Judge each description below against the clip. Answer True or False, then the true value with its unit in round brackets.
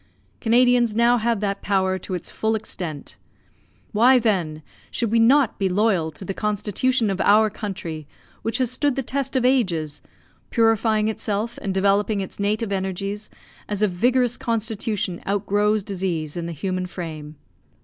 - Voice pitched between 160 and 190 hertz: False (210 Hz)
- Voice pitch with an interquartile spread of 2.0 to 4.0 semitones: True (3.4 semitones)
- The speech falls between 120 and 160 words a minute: True (155 wpm)